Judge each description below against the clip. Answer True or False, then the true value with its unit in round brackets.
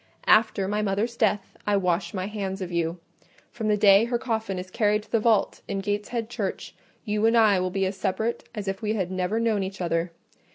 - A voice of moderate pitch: False (205 Hz)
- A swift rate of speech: True (215 wpm)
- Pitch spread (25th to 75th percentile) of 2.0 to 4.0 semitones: True (2.6 semitones)